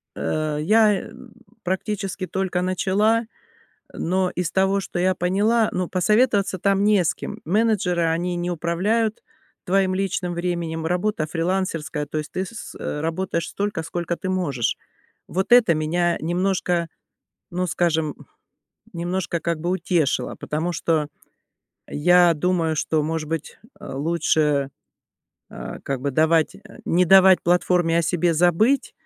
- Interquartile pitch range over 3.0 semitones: No, narrow, 2.6 semitones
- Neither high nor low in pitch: Yes, medium, 175 Hz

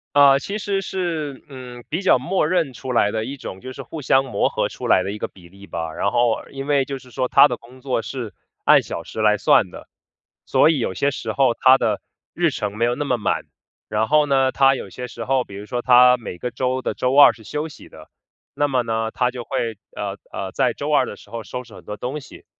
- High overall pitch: No, low, 125 Hz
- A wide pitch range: No, average, 3.7 semitones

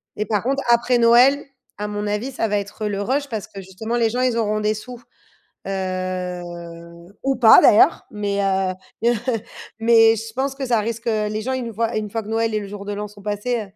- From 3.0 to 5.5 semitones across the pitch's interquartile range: No, narrow, 2.5 semitones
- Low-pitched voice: No, high, 220 Hz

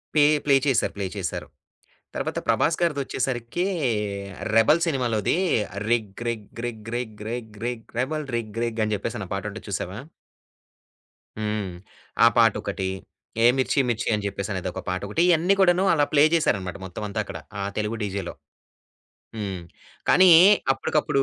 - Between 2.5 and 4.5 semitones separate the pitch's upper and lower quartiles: No, average, 4.9 semitones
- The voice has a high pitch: No, low, 115 Hz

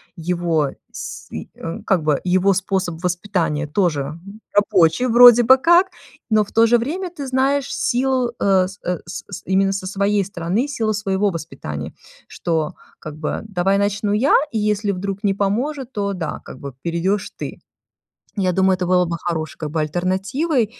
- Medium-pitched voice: No, high, 195 Hz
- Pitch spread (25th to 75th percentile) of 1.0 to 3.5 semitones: No, average, 4.3 semitones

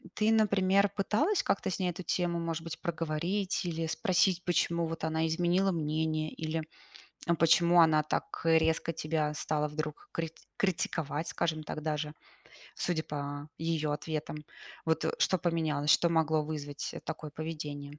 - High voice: No, medium, 160 Hz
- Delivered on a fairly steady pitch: Yes, narrow, 2.1 semitones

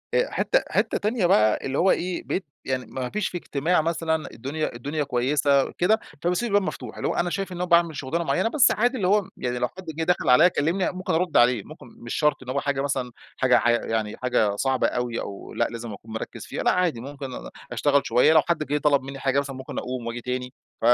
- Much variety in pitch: Yes, wide, 5.9 semitones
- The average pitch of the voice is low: No, medium, 145 Hz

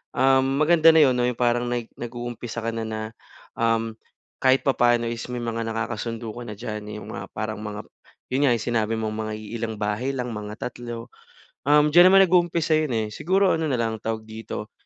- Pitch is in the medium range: No, low, 120 Hz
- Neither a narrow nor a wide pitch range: Yes, average, 3.1 semitones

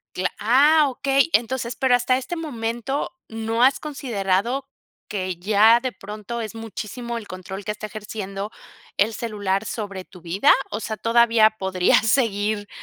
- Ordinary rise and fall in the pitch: Yes, average, 3.3 semitones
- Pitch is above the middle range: Yes, high, 225 Hz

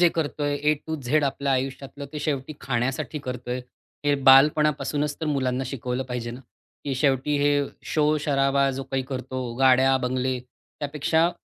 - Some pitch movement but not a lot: No, narrow, 2.3 semitones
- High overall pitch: No, low, 135 Hz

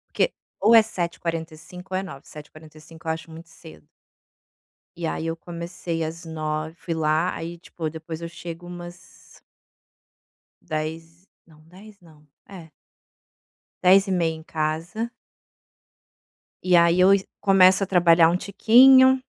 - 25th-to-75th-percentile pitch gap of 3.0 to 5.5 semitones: No, narrow, 2.4 semitones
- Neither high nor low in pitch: Yes, medium, 170 Hz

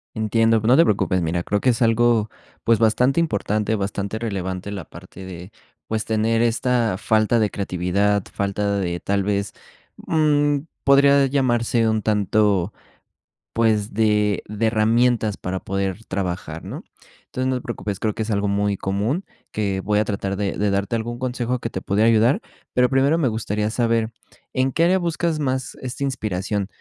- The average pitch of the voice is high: No, low, 110 Hz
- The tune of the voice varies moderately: Yes, average, 3.1 semitones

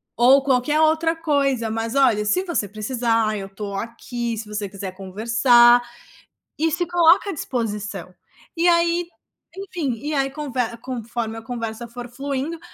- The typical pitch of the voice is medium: No, high, 245 Hz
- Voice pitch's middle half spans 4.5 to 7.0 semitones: Yes, average, 5.3 semitones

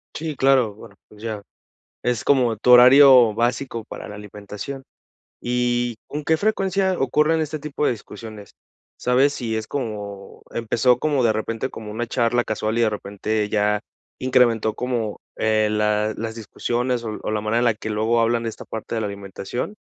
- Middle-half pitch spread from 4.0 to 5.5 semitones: No, average, 2.9 semitones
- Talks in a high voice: No, low, 115 Hz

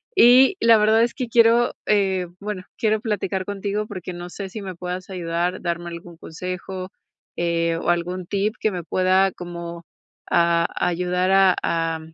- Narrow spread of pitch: No, average, 3.1 semitones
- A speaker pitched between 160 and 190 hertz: Yes, medium, 185 Hz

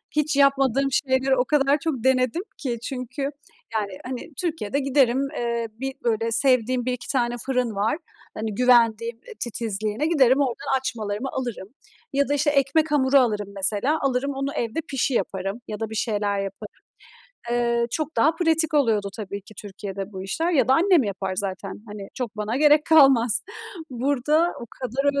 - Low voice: No, very high, 250 Hz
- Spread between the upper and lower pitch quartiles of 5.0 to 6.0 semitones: No, average, 4.2 semitones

